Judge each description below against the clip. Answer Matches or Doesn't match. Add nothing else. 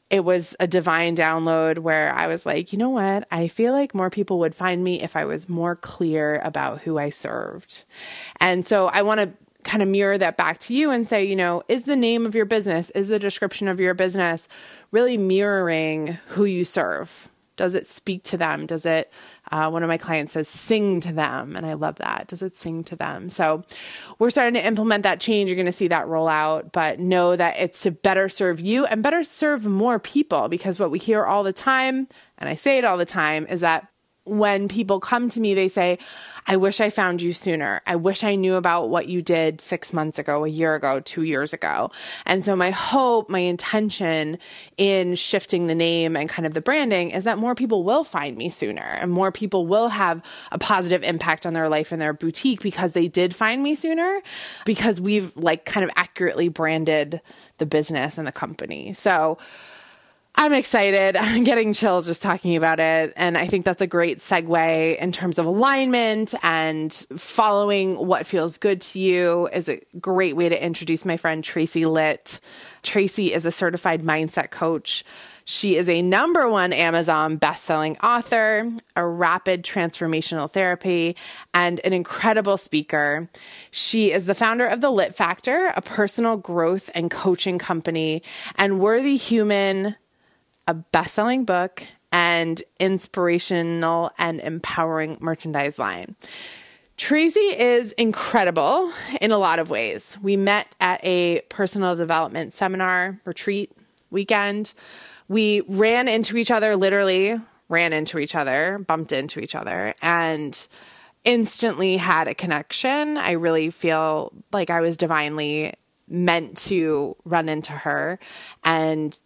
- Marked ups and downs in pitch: Doesn't match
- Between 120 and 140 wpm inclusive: Doesn't match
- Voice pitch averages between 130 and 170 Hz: Doesn't match